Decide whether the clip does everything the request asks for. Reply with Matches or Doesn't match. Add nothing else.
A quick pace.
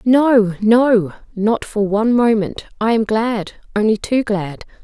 Doesn't match